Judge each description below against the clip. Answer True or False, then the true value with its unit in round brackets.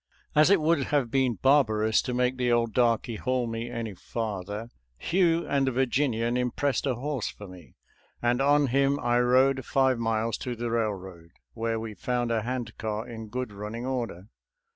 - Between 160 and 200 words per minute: True (190 wpm)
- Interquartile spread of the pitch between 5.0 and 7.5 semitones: False (3.0 semitones)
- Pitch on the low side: True (120 Hz)